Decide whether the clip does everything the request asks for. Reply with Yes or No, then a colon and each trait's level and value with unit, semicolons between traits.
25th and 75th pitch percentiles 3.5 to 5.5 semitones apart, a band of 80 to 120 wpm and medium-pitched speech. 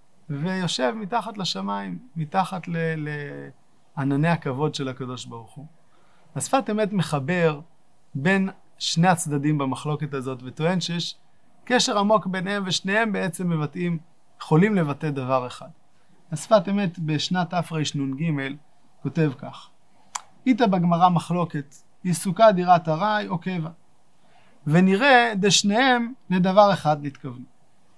Yes: average, 4.5 semitones; average, 105 wpm; medium, 170 Hz